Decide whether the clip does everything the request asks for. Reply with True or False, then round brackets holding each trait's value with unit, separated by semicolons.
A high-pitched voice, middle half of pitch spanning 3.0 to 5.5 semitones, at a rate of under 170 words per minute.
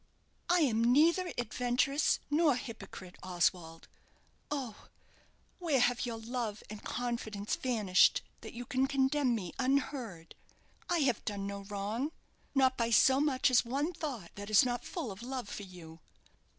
True (245 Hz; 4.8 semitones; 150 wpm)